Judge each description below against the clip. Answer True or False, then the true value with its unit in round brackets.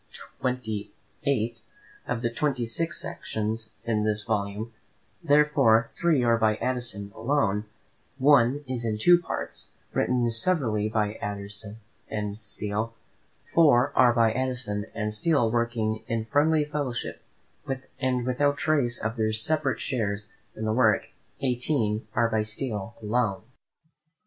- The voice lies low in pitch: True (115 Hz)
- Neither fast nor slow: False (125 wpm)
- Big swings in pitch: False (3.3 semitones)